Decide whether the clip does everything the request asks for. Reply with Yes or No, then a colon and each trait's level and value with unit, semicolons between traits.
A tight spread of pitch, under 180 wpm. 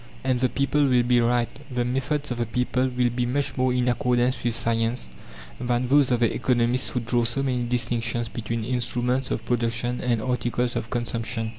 No: narrow, 1.2 semitones; average, 190 wpm